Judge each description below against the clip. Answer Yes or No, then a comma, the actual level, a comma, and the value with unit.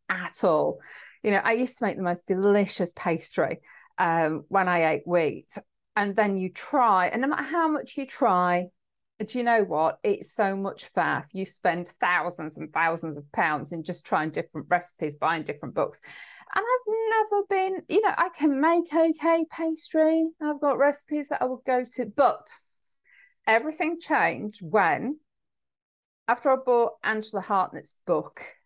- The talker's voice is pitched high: Yes, high, 225 Hz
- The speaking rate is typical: Yes, average, 170 wpm